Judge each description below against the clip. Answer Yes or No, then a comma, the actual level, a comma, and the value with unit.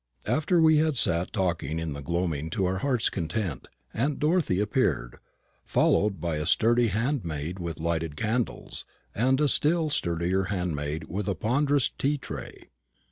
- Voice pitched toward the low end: Yes, very low, 95 Hz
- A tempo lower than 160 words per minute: Yes, average, 150 wpm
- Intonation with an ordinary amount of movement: No, wide, 8.0 semitones